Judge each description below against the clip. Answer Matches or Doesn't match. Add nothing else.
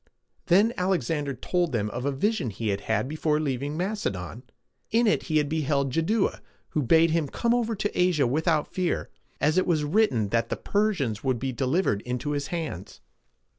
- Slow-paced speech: Doesn't match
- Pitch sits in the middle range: Matches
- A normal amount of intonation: Doesn't match